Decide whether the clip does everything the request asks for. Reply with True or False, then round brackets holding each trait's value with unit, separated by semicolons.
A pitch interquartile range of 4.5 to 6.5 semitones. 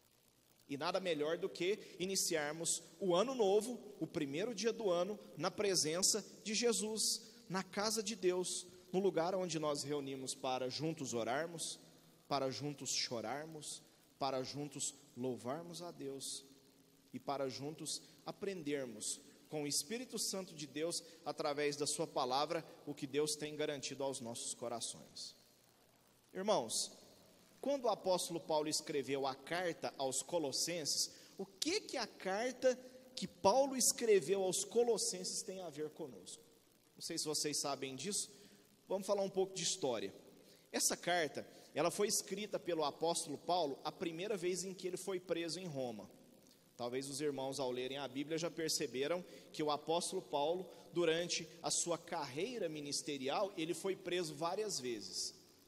True (4.8 semitones)